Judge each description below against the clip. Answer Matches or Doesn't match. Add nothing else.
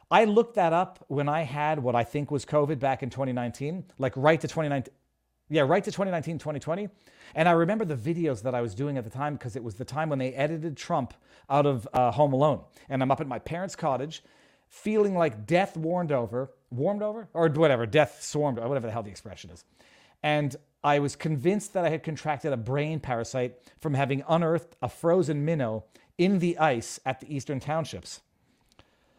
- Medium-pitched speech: Matches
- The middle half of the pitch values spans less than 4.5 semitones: Matches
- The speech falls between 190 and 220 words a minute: Matches